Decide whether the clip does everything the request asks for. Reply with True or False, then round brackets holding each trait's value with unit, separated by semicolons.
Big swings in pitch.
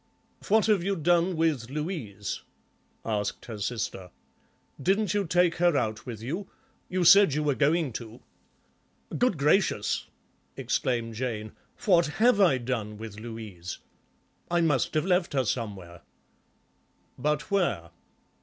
True (7.8 semitones)